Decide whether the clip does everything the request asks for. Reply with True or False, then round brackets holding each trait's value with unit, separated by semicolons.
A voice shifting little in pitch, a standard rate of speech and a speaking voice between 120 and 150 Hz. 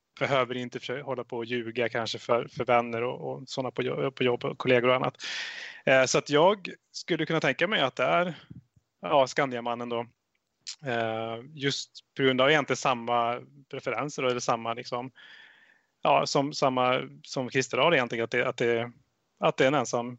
True (2.3 semitones; 180 wpm; 125 Hz)